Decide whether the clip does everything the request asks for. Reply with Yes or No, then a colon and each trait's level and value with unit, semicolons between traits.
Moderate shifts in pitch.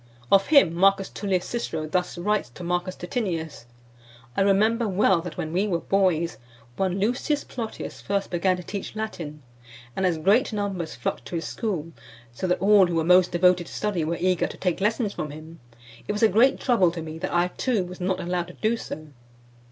Yes: average, 3.4 semitones